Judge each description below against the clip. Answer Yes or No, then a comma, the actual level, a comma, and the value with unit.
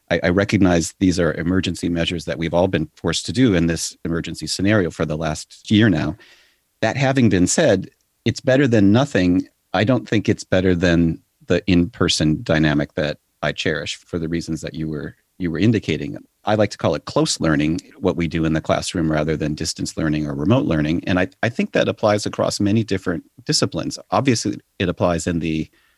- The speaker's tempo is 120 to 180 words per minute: No, average, 200 wpm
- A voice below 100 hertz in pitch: Yes, very low, 90 Hz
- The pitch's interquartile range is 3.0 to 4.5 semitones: Yes, average, 3.7 semitones